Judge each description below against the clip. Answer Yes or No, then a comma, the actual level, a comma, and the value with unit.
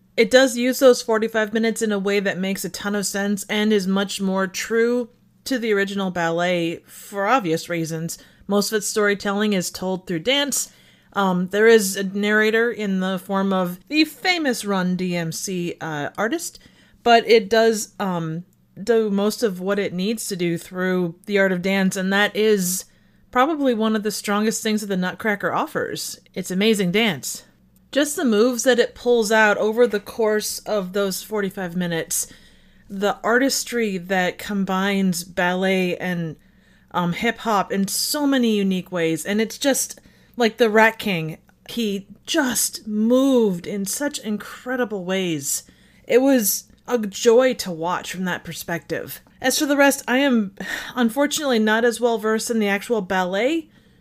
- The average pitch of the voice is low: No, high, 205 Hz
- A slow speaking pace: No, average, 165 wpm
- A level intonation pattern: No, average, 3.6 semitones